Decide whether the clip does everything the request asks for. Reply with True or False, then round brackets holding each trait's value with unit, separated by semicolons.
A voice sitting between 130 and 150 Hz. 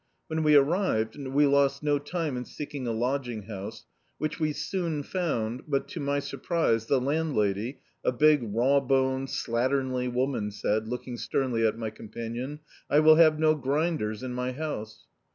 True (135 Hz)